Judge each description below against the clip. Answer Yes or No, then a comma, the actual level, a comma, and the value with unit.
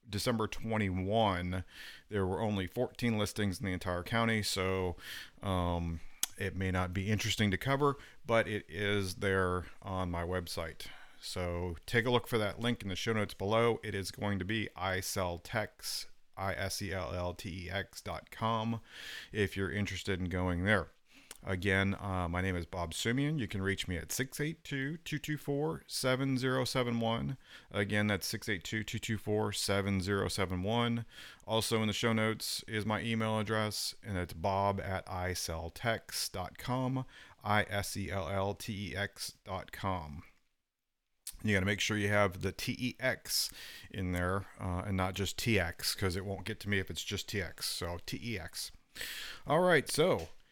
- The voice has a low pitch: Yes, low, 100 Hz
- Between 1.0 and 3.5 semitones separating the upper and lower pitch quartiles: Yes, average, 3.2 semitones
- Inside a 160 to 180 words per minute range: No, average, 145 wpm